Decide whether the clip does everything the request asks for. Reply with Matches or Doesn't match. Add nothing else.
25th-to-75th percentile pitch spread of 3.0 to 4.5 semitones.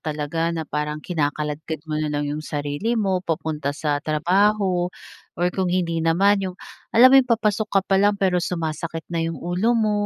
Matches